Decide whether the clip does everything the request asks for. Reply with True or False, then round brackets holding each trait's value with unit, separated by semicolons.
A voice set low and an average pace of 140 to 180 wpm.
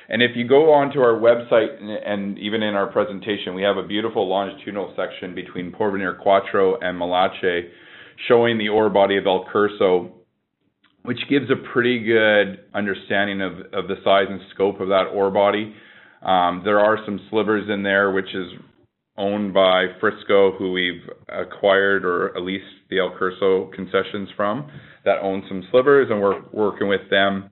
True (100 Hz; 170 wpm)